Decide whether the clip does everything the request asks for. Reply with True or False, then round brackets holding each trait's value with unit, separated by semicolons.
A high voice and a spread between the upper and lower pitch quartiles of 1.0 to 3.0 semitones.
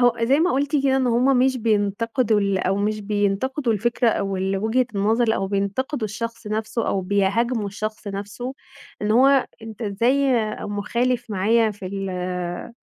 False (220 Hz; 3.6 semitones)